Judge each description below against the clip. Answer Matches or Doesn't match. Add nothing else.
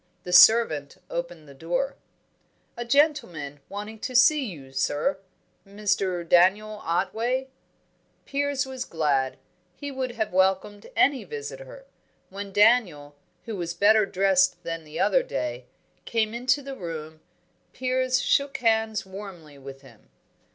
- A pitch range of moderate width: Doesn't match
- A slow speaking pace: Matches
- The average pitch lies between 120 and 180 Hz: Doesn't match